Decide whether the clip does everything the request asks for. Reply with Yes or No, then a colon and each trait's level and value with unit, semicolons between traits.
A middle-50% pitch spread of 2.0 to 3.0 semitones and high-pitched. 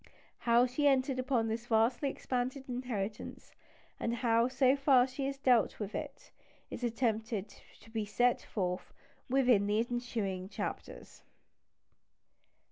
Yes: narrow, 2.6 semitones; high, 240 Hz